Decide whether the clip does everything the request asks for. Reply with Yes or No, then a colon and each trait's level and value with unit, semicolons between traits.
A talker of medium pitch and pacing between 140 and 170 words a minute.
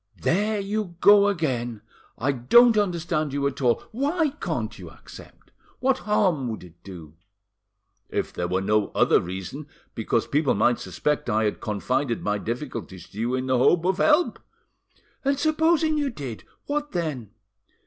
Yes: medium, 145 Hz; average, 160 wpm